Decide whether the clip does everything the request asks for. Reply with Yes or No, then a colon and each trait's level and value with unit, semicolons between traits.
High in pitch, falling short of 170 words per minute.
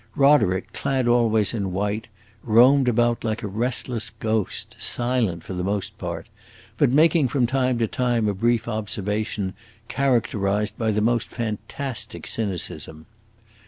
No: low, 110 Hz; slow, 135 wpm